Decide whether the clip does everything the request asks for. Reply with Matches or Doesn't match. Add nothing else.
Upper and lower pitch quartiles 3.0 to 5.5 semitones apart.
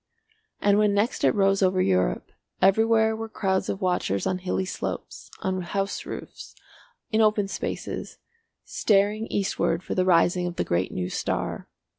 Doesn't match